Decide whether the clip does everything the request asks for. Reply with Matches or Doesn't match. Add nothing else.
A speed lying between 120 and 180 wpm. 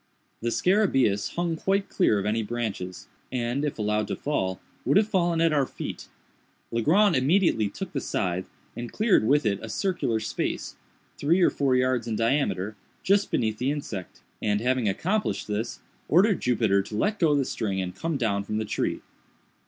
Matches